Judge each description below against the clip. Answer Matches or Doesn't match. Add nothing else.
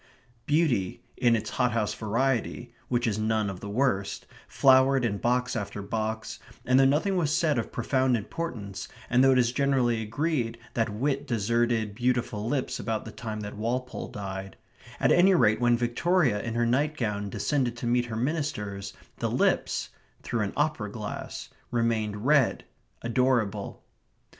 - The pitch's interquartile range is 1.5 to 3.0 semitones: Doesn't match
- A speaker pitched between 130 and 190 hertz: Doesn't match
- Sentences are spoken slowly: Doesn't match